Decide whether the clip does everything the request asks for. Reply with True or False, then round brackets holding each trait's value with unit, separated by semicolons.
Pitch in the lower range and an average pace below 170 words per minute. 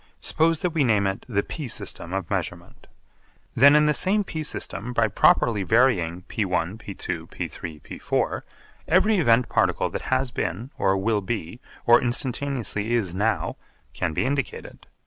True (115 Hz; 155 wpm)